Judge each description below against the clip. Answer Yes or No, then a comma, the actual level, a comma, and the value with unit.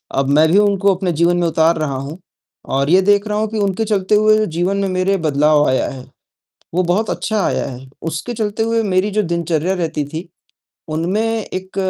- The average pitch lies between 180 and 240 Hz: Yes, medium, 185 Hz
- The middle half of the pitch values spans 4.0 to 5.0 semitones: Yes, average, 4.6 semitones